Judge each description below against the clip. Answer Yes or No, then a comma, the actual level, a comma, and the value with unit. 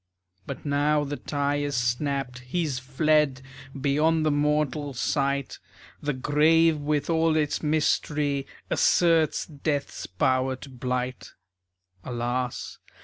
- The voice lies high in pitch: No, medium, 145 Hz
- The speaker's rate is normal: No, slow, 110 wpm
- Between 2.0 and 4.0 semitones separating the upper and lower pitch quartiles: Yes, narrow, 2.6 semitones